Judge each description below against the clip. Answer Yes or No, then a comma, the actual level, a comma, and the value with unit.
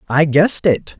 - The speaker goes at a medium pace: Yes, average, 180 wpm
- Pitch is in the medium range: Yes, medium, 155 Hz